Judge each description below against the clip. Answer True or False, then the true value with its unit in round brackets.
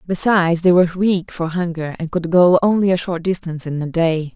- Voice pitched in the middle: True (175 Hz)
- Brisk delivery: True (220 wpm)